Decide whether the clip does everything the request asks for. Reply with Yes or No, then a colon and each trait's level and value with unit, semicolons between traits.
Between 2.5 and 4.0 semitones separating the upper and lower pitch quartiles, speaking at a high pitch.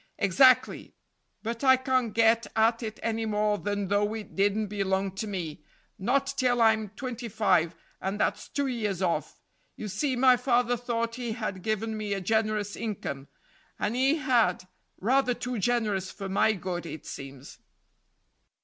Yes: average, 3.6 semitones; high, 220 Hz